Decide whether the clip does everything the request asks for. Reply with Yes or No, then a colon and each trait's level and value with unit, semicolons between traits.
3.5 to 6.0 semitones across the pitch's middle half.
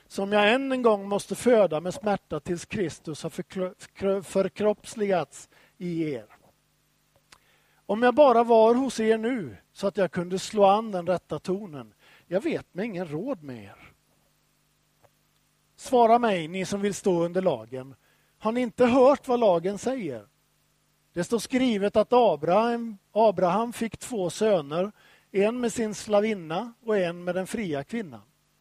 Yes: average, 4.0 semitones